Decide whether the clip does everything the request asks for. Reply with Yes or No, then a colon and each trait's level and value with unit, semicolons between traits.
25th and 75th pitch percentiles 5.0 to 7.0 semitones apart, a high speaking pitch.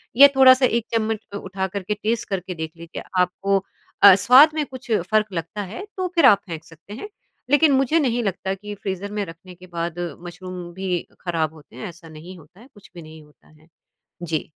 Yes: wide, 5.4 semitones; high, 195 Hz